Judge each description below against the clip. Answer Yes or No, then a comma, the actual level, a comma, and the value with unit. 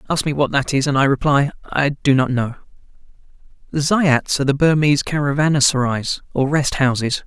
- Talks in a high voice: No, medium, 140 Hz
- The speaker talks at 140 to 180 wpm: Yes, average, 175 wpm